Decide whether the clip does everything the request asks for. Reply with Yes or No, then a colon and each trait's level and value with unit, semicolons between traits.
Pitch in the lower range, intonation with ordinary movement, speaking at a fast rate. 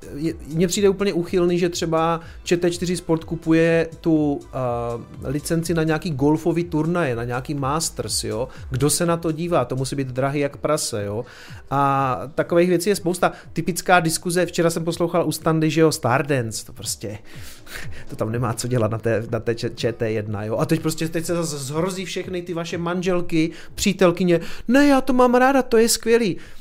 No: medium, 160 Hz; average, 4.4 semitones; fast, 180 wpm